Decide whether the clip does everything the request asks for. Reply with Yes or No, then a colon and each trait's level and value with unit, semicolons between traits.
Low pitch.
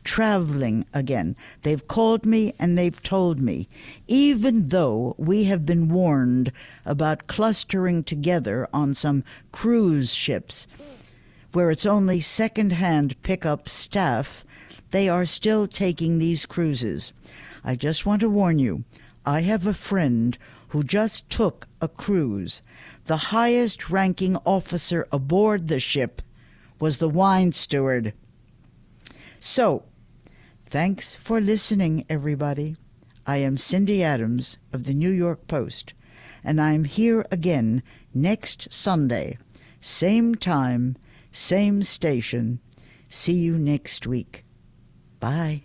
No: medium, 155 Hz